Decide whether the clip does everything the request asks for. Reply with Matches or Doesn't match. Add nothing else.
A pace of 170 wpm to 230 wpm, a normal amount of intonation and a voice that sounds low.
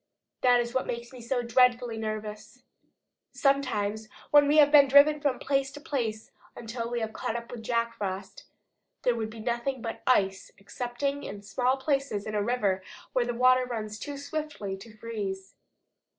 Doesn't match